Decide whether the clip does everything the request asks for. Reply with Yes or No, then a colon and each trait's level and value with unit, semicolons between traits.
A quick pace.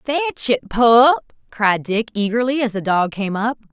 No: average, 175 wpm